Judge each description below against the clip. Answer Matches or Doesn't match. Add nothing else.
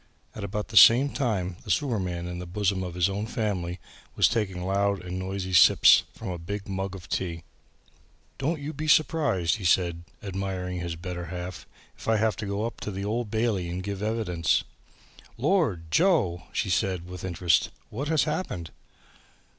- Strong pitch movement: Doesn't match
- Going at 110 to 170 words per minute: Doesn't match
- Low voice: Matches